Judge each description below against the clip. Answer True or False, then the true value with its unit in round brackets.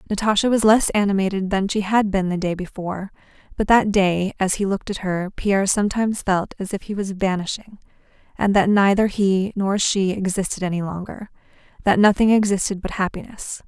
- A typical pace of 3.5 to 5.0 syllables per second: False (5.6 syllables/s)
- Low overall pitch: False (195 Hz)